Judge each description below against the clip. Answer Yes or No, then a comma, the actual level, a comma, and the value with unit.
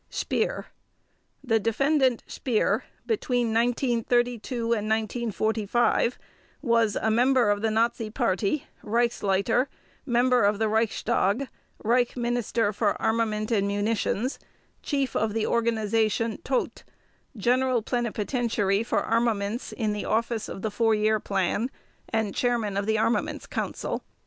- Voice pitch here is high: Yes, high, 225 Hz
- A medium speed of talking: No, slow, 120 wpm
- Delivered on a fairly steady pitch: Yes, narrow, 2.2 semitones